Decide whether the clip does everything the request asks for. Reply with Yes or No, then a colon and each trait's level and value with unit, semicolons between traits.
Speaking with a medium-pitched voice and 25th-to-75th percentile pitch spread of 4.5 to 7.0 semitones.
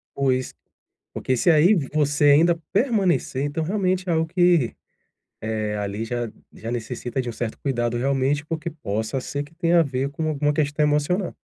Yes: medium, 145 Hz; average, 4.8 semitones